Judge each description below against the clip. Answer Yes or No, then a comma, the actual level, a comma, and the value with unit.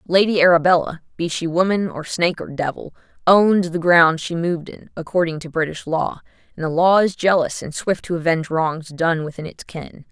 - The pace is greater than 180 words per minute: Yes, average, 195 wpm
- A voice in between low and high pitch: Yes, medium, 170 Hz